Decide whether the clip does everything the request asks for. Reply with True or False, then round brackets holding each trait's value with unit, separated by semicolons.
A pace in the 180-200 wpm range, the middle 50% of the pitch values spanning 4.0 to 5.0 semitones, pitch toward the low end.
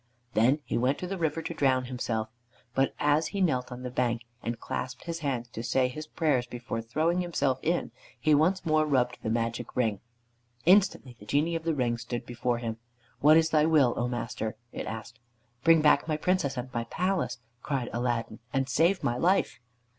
True (195 wpm; 4.7 semitones; 130 Hz)